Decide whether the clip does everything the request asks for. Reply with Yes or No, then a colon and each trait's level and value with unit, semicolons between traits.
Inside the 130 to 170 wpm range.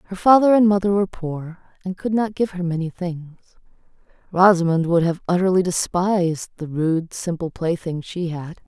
Yes: average, 165 wpm